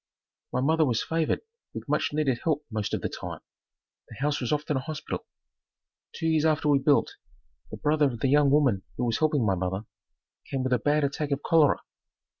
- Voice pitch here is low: No, medium, 145 Hz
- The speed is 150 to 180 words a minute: No, average, 200 wpm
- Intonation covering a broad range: No, average, 3.3 semitones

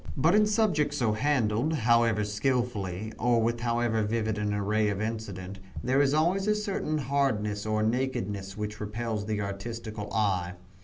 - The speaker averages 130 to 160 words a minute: Yes, average, 155 wpm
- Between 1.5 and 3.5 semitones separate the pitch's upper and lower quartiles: No, average, 4.0 semitones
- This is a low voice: Yes, low, 110 Hz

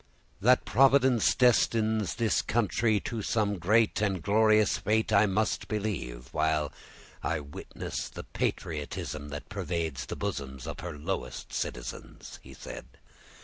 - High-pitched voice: No, low, 100 Hz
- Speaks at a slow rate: Yes, slow, 130 wpm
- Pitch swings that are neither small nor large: No, wide, 6.3 semitones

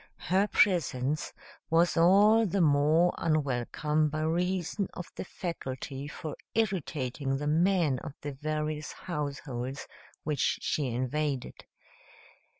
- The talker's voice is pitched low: No, medium, 155 Hz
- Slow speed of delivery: Yes, slow, 110 wpm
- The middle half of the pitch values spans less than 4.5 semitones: Yes, average, 3.8 semitones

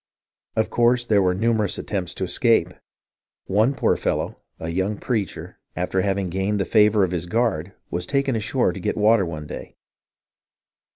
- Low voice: Yes, low, 100 Hz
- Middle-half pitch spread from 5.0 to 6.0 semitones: No, average, 3.7 semitones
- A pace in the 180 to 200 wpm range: No, average, 165 wpm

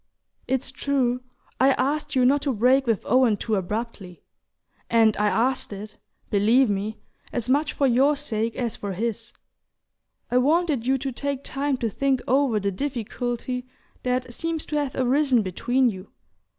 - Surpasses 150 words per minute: Yes, average, 160 wpm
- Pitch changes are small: No, average, 3.6 semitones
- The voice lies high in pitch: Yes, very high, 250 Hz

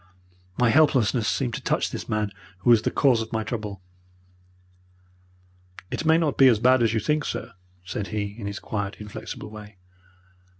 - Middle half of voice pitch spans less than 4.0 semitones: Yes, average, 3.4 semitones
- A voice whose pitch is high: No, low, 110 Hz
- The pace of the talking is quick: No, average, 175 wpm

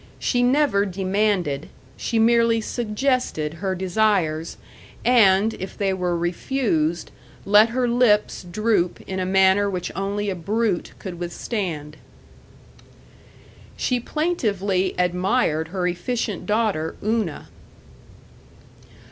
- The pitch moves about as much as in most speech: Yes, average, 4.2 semitones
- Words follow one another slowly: Yes, slow, 105 wpm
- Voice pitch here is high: Yes, high, 195 Hz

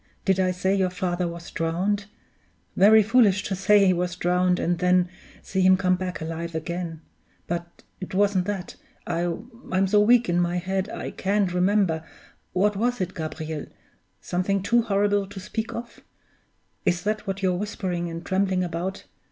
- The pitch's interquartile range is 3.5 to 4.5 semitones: No, narrow, 2.4 semitones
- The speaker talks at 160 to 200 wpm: Yes, average, 165 wpm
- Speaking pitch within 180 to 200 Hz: Yes, medium, 185 Hz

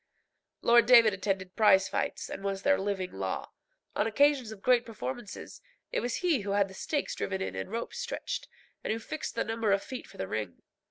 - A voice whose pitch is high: Yes, high, 215 Hz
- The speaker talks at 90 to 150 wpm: No, fast, 205 wpm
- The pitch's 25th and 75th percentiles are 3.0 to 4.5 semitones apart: Yes, average, 4.0 semitones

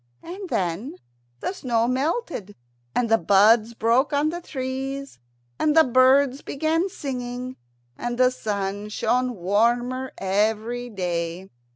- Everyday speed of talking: No, slow, 120 wpm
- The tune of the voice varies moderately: Yes, average, 4.4 semitones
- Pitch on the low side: No, high, 245 Hz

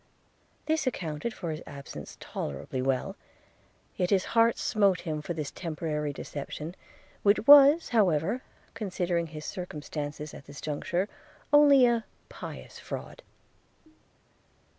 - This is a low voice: No, medium, 175 Hz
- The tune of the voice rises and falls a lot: Yes, wide, 6.6 semitones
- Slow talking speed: Yes, slow, 120 wpm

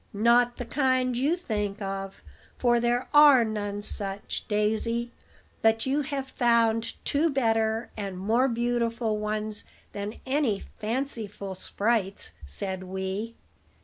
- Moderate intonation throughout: Yes, average, 3.0 semitones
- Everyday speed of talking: No, slow, 120 wpm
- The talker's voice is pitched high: Yes, high, 225 Hz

